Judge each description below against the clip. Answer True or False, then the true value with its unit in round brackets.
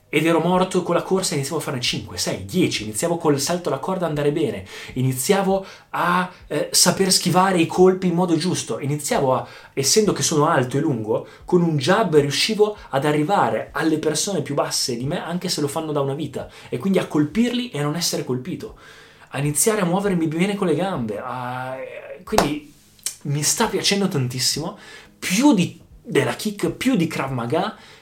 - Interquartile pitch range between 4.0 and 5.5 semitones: True (4.5 semitones)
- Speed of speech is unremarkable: False (190 wpm)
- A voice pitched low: False (160 Hz)